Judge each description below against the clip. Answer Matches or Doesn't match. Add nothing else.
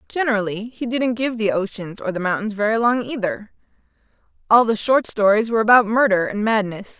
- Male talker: Doesn't match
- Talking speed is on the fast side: Doesn't match